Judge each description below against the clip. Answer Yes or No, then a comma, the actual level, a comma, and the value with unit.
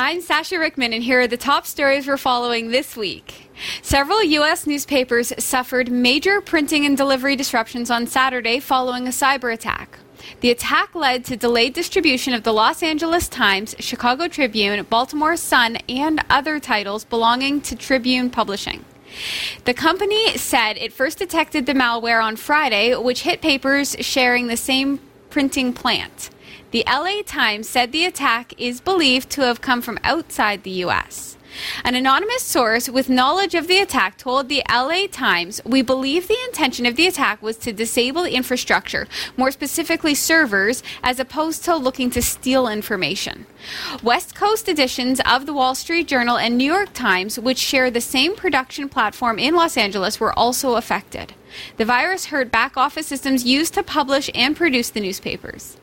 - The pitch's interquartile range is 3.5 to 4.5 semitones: Yes, average, 4.1 semitones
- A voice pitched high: Yes, very high, 260 Hz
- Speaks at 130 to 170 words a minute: Yes, average, 165 wpm